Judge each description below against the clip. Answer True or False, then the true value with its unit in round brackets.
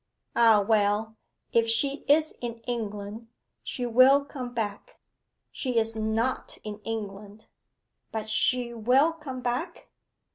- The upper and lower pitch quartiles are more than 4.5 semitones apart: False (2.8 semitones)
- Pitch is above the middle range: True (230 Hz)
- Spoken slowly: True (120 wpm)